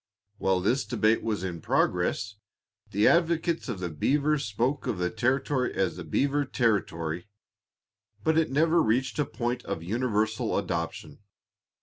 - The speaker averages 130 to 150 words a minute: Yes, average, 140 wpm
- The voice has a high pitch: No, low, 115 Hz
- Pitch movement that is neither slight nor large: No, wide, 6.9 semitones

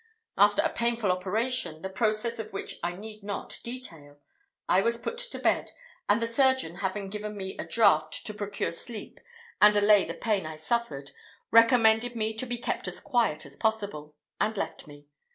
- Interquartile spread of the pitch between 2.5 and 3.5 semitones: No, average, 4.1 semitones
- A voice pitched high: Yes, high, 210 Hz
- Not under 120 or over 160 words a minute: No, average, 180 wpm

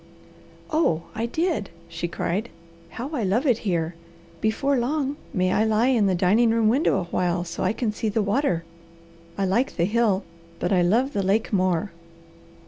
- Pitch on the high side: Yes, high, 215 Hz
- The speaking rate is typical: Yes, average, 180 wpm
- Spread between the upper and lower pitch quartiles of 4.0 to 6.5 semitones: Yes, average, 4.6 semitones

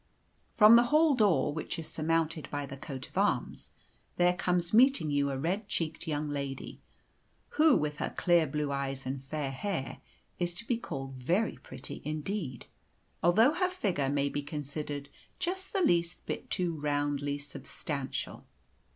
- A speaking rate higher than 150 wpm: Yes, average, 160 wpm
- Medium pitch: Yes, medium, 155 Hz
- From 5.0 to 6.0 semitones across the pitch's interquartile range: Yes, average, 5.3 semitones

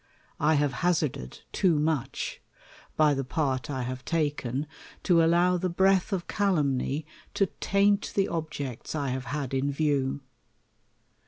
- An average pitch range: Yes, average, 4.4 semitones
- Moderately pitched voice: Yes, medium, 150 Hz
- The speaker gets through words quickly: No, average, 145 wpm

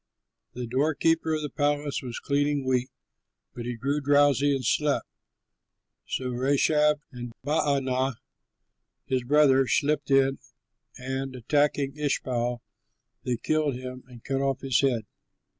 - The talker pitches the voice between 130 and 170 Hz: Yes, low, 135 Hz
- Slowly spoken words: Yes, slow, 125 wpm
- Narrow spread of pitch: Yes, narrow, 2.3 semitones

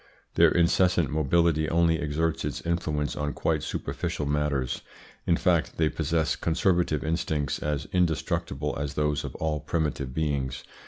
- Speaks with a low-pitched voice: Yes, very low, 75 Hz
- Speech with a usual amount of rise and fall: No, narrow, 2.3 semitones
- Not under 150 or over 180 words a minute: No, average, 140 wpm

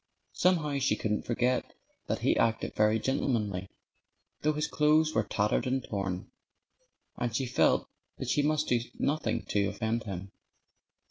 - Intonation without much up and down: No, wide, 5.6 semitones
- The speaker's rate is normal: Yes, average, 145 wpm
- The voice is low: Yes, low, 120 Hz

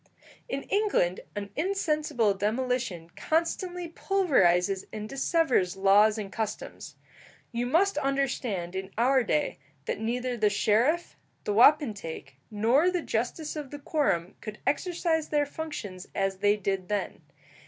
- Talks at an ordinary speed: No, slow, 130 wpm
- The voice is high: Yes, high, 235 Hz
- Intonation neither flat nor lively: No, wide, 7.3 semitones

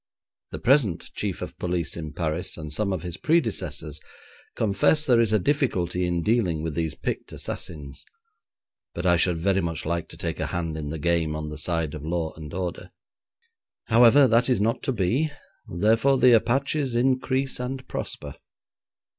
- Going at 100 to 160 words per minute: No, average, 170 wpm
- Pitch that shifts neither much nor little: No, wide, 6.6 semitones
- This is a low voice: Yes, very low, 90 Hz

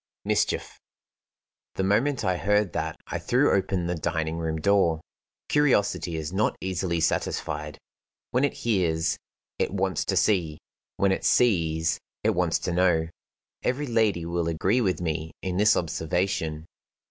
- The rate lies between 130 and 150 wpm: Yes, average, 145 wpm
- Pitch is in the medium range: No, very low, 90 Hz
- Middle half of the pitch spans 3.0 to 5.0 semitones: Yes, average, 3.9 semitones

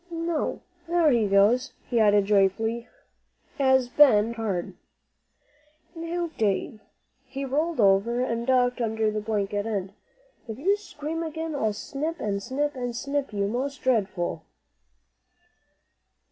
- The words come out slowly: Yes, slow, 130 wpm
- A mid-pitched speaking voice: No, high, 240 Hz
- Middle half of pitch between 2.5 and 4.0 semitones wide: No, wide, 5.6 semitones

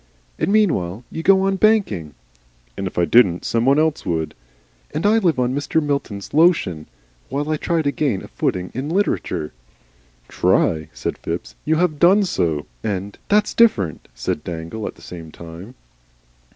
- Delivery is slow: No, average, 165 wpm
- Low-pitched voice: Yes, low, 125 Hz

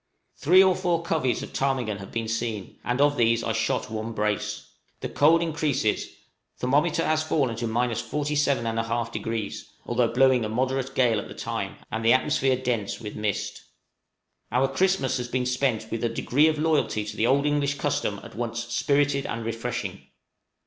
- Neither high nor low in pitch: No, low, 125 Hz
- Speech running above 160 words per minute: Yes, average, 175 wpm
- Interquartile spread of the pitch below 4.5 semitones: Yes, average, 4.0 semitones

